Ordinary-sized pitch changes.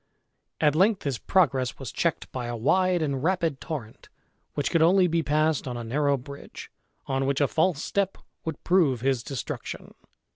Yes: average, 4.1 semitones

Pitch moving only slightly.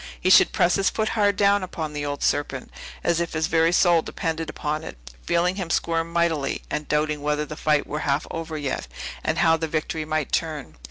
Yes: narrow, 2.2 semitones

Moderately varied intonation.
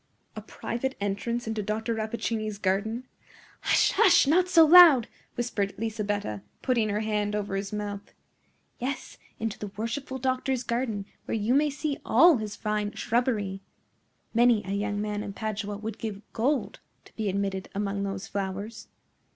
Yes: average, 3.0 semitones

